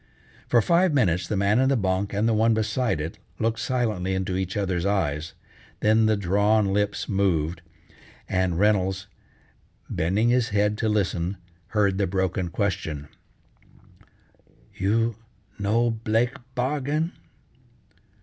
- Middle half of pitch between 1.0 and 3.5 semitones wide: Yes, average, 3.2 semitones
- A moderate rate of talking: No, slow, 130 wpm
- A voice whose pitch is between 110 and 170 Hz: No, low, 100 Hz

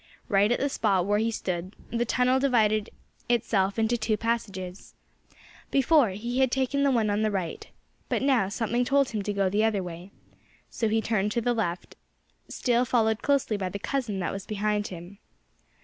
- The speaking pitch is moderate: No, high, 220 Hz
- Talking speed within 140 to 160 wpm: No, average, 185 wpm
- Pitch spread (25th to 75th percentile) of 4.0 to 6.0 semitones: No, average, 3.4 semitones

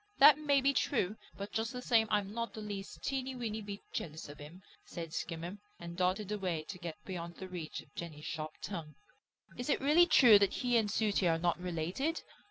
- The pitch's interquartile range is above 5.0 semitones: Yes, wide, 5.4 semitones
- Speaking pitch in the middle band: No, high, 200 Hz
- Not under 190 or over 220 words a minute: Yes, fast, 205 wpm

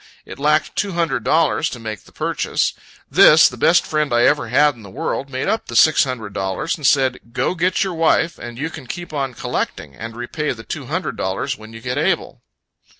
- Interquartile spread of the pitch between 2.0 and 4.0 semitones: No, average, 5.0 semitones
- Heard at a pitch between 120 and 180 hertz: Yes, low, 135 Hz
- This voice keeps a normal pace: No, fast, 215 wpm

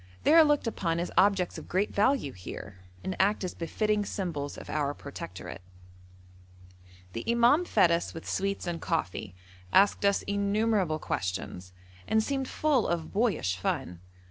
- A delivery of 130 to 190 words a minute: Yes, average, 150 wpm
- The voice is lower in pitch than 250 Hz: Yes, high, 190 Hz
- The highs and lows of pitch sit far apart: Yes, wide, 5.8 semitones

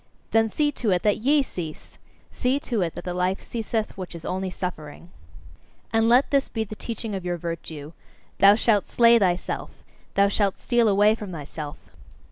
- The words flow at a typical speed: Yes, average, 180 wpm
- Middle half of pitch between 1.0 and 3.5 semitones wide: No, average, 4.2 semitones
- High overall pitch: Yes, high, 200 Hz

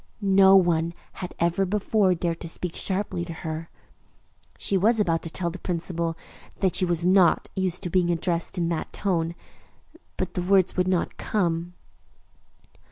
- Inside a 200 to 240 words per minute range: No, average, 165 wpm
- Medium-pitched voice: Yes, medium, 175 Hz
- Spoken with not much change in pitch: Yes, narrow, 2.1 semitones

